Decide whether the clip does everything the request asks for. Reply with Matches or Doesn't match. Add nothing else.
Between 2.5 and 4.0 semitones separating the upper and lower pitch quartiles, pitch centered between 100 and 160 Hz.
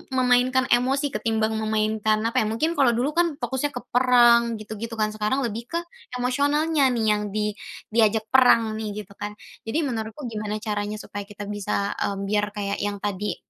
Doesn't match